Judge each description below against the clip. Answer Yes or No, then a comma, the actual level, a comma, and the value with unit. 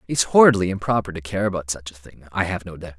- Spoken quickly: Yes, fast, 260 wpm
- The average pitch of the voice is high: No, very low, 95 Hz